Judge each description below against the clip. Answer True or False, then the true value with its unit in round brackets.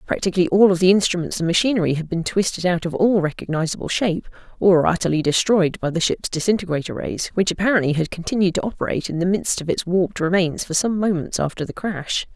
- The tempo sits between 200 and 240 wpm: True (205 wpm)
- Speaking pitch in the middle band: True (180 Hz)